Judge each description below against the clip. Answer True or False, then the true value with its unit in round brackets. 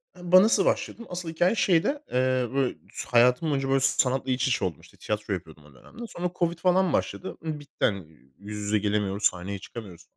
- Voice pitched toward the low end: True (130 Hz)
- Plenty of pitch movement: True (9.0 semitones)